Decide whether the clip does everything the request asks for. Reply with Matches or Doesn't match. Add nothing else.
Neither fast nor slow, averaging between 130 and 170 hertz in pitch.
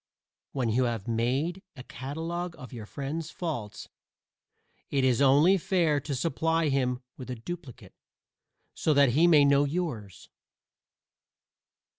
Doesn't match